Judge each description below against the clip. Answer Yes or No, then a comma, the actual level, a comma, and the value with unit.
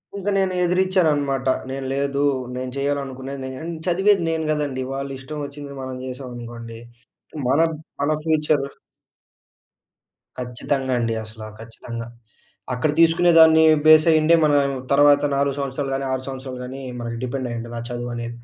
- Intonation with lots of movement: No, average, 3.4 semitones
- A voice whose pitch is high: No, low, 135 Hz